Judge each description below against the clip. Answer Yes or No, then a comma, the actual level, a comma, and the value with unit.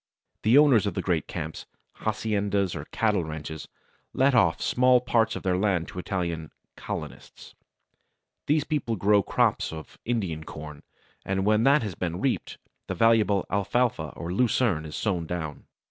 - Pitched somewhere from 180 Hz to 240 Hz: No, low, 100 Hz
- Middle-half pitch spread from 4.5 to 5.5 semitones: Yes, average, 5.2 semitones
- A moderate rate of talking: Yes, average, 155 wpm